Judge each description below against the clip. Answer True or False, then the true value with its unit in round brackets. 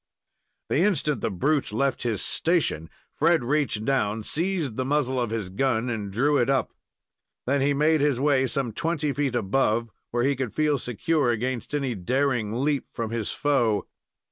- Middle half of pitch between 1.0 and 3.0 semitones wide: False (4.2 semitones)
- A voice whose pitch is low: True (130 Hz)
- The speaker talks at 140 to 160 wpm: False (170 wpm)